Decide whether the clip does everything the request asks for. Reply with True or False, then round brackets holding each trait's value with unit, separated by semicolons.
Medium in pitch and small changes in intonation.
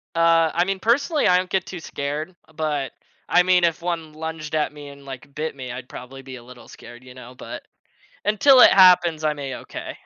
False (155 Hz; 4.7 semitones)